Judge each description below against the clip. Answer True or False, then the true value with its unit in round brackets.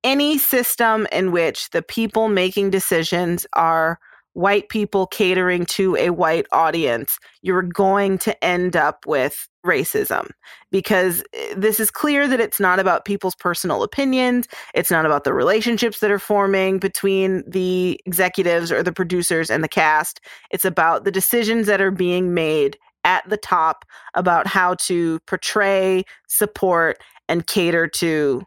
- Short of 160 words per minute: True (150 wpm)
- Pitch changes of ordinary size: True (3.0 semitones)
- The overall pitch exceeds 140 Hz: True (190 Hz)